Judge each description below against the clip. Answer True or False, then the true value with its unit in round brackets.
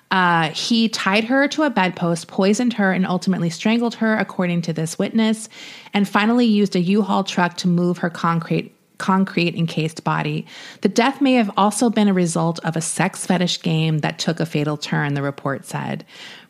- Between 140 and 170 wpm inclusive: False (185 wpm)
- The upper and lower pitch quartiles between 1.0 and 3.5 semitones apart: False (4.3 semitones)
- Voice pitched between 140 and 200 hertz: True (185 Hz)